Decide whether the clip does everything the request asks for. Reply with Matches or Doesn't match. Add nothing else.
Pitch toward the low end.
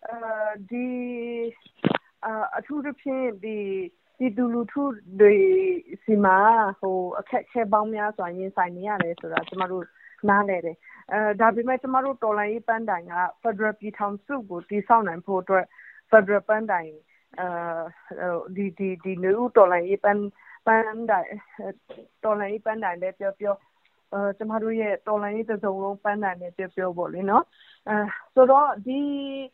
Doesn't match